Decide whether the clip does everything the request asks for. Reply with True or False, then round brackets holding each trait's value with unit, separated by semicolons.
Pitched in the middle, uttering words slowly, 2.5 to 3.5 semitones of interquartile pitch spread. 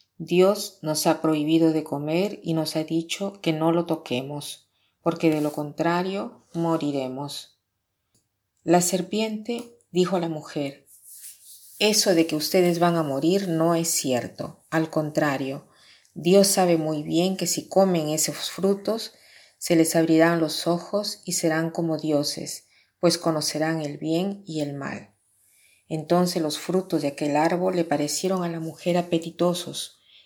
False (165 Hz; 145 wpm; 2.9 semitones)